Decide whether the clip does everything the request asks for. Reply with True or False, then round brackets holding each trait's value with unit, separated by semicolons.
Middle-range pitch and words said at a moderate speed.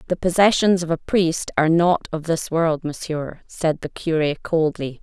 True (165 Hz; 180 wpm)